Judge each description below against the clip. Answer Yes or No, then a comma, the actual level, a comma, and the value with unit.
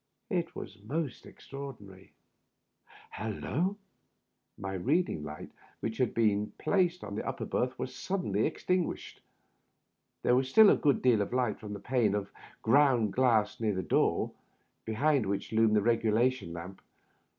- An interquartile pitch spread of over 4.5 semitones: Yes, average, 4.9 semitones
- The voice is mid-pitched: No, low, 115 Hz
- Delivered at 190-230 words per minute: No, average, 150 wpm